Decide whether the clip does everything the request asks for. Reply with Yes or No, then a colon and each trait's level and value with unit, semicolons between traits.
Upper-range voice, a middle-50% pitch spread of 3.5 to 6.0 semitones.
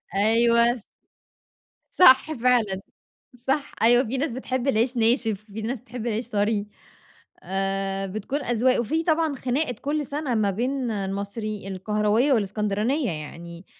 Yes: high, 230 Hz; average, 4.2 semitones